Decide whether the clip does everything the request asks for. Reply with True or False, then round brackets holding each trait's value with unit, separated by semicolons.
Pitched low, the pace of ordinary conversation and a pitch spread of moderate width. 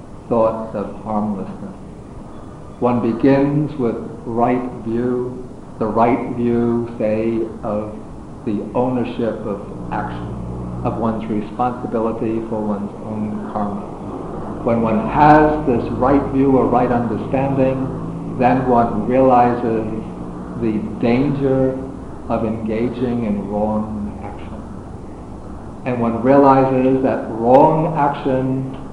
False (115 Hz; 100 wpm; 3.3 semitones)